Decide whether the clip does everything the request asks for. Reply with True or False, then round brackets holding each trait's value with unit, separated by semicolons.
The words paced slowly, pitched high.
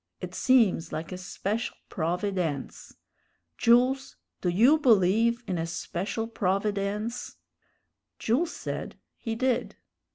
True (105 wpm; 210 Hz)